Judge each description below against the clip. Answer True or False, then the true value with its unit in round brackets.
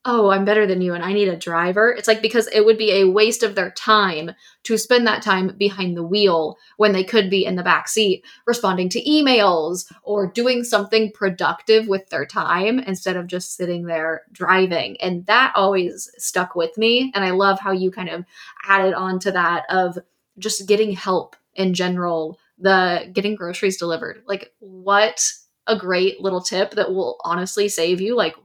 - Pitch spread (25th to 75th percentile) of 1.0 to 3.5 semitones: True (2.9 semitones)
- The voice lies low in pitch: False (195 Hz)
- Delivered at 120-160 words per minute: False (190 wpm)